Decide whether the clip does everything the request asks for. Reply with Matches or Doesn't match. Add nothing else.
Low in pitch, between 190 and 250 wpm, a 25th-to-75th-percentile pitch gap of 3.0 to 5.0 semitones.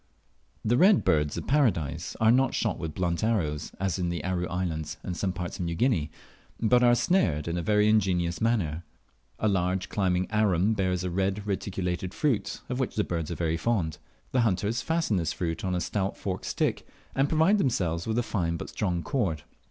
Matches